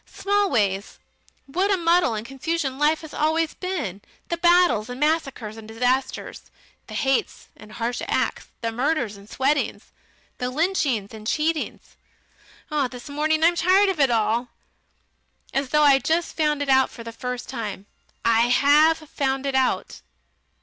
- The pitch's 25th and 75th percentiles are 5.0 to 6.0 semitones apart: Yes, average, 5.3 semitones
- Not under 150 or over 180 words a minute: Yes, average, 155 wpm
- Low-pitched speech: No, very high, 270 Hz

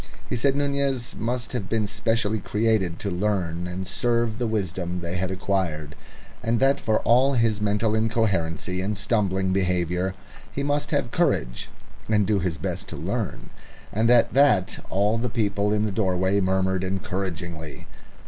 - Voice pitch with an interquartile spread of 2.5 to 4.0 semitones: Yes, average, 3.6 semitones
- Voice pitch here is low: Yes, low, 100 Hz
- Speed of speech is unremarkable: Yes, average, 160 wpm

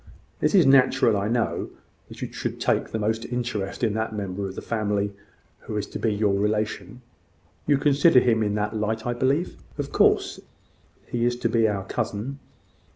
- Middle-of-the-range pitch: No, low, 110 Hz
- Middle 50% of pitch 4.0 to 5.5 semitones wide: No, average, 2.9 semitones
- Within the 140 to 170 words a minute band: No, average, 185 wpm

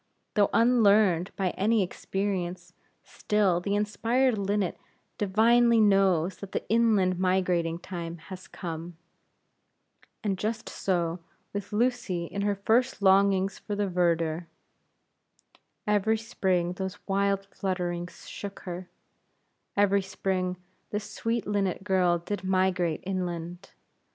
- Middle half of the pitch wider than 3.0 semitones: No, narrow, 2.6 semitones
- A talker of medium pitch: No, high, 195 Hz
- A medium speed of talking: No, slow, 115 wpm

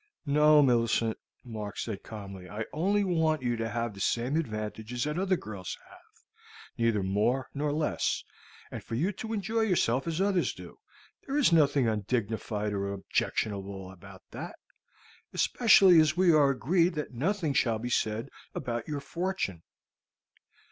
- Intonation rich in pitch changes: Yes, wide, 7.3 semitones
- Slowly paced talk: No, average, 150 wpm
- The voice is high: No, low, 125 Hz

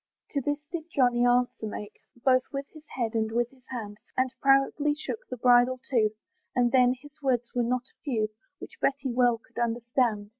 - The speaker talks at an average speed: Yes, average, 190 wpm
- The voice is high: Yes, high, 245 Hz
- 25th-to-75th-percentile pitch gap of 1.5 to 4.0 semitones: Yes, narrow, 2.4 semitones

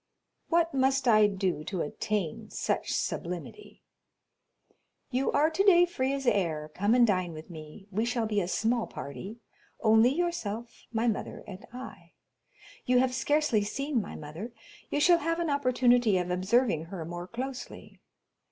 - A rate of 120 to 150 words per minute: Yes, average, 145 wpm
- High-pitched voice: Yes, high, 230 Hz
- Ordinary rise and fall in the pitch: No, wide, 6.3 semitones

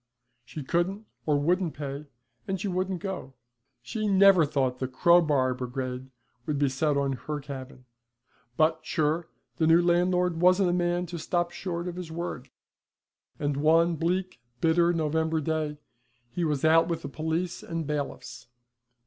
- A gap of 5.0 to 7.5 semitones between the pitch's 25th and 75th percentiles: No, average, 3.4 semitones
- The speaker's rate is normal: Yes, average, 155 wpm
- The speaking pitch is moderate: Yes, medium, 160 Hz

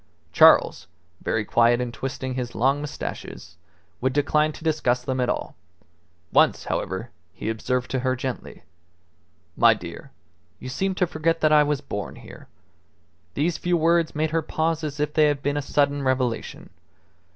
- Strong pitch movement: No, average, 3.6 semitones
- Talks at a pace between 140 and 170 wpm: Yes, average, 165 wpm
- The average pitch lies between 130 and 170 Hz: Yes, medium, 140 Hz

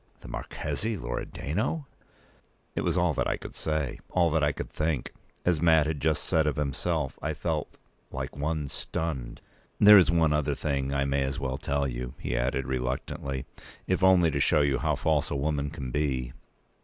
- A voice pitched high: No, very low, 75 Hz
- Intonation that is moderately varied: Yes, average, 3.0 semitones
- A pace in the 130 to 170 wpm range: No, average, 185 wpm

